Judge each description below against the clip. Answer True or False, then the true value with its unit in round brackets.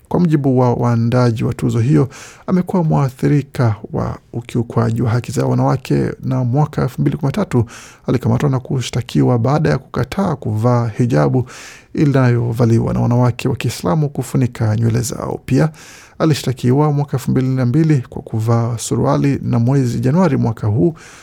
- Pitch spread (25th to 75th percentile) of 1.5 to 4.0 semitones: True (3.4 semitones)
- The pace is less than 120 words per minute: False (135 wpm)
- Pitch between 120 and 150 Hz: True (125 Hz)